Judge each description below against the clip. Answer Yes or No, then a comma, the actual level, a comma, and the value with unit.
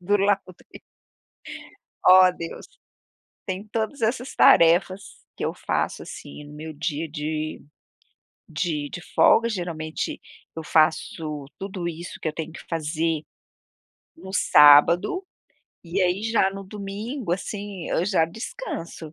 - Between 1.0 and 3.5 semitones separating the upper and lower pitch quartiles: No, average, 3.9 semitones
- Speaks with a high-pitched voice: No, medium, 175 Hz